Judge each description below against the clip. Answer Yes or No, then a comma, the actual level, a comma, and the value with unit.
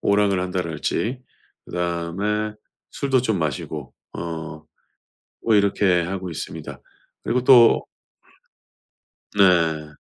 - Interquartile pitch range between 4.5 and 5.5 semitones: No, average, 4.0 semitones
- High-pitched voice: No, very low, 95 Hz